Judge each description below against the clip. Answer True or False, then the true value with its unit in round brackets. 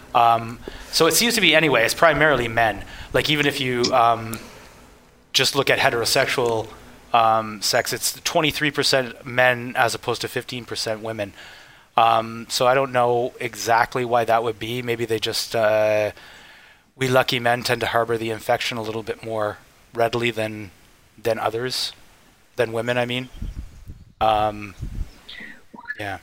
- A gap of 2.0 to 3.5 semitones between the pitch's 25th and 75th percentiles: True (2.4 semitones)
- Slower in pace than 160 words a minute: True (150 wpm)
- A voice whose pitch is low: True (115 Hz)